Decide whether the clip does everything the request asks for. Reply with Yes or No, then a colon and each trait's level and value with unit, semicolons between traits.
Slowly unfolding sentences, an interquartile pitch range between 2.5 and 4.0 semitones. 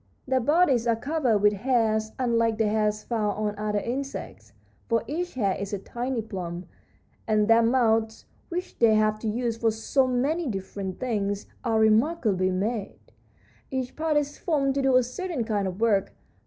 No: average, 170 wpm; average, 3.6 semitones